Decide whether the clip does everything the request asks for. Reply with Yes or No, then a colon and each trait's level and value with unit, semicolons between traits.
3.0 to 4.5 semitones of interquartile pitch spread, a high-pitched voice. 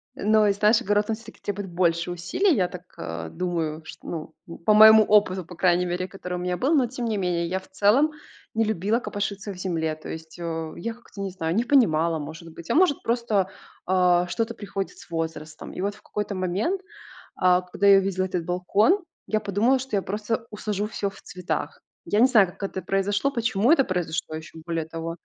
Yes: average, 3.7 semitones; high, 195 Hz